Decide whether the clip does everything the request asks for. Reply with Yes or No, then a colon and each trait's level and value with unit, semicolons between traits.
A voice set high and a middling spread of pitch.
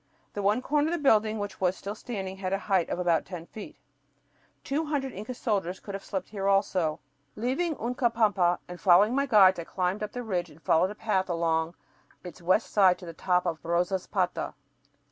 Yes: high, 195 Hz; average, 3.6 semitones